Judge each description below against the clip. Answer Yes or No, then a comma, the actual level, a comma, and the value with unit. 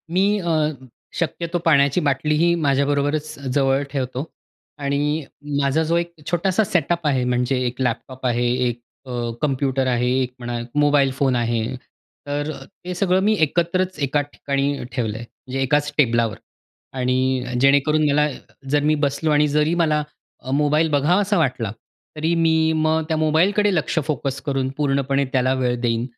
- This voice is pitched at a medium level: Yes, medium, 145 Hz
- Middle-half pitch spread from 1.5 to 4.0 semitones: Yes, average, 3.2 semitones